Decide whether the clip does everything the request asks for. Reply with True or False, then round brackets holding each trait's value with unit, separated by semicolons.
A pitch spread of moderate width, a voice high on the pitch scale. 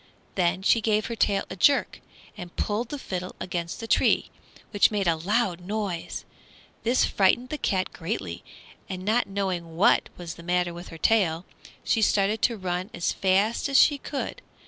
True (3.9 semitones; 195 Hz)